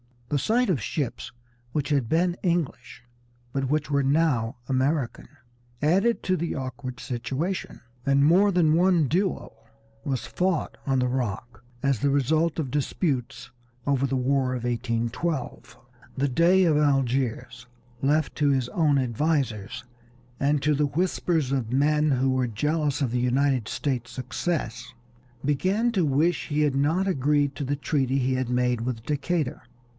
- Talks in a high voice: No, medium, 140 Hz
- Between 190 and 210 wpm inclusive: No, average, 150 wpm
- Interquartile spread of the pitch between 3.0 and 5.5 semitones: Yes, average, 3.7 semitones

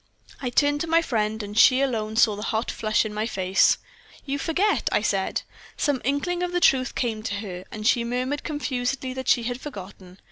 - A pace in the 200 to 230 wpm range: Yes, fast, 205 wpm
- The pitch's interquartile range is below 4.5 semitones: No, average, 4.8 semitones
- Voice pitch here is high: Yes, high, 245 Hz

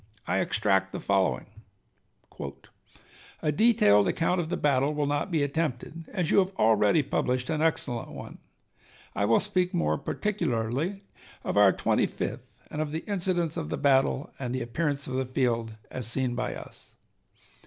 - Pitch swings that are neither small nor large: No, wide, 5.9 semitones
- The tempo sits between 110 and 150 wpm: No, average, 165 wpm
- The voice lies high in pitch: No, medium, 140 Hz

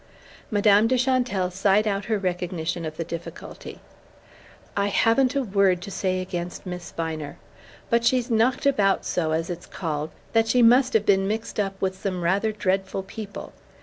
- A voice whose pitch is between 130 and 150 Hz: No, high, 195 Hz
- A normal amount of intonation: Yes, average, 3.8 semitones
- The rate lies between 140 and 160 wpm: No, average, 170 wpm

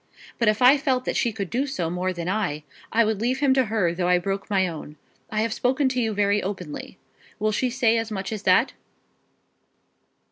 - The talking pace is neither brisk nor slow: No, fast, 215 wpm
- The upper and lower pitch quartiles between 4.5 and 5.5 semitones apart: Yes, average, 4.8 semitones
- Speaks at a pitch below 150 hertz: No, high, 215 Hz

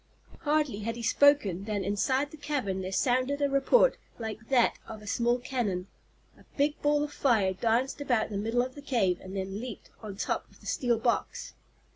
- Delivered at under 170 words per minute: No, average, 195 wpm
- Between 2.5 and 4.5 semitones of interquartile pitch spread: No, average, 5.3 semitones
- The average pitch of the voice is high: Yes, high, 240 Hz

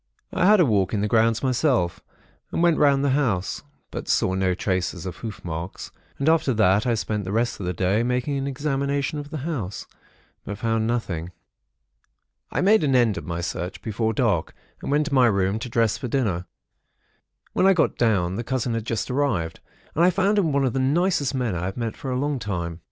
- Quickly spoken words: Yes, fast, 215 wpm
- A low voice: Yes, low, 115 Hz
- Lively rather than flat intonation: Yes, wide, 6.2 semitones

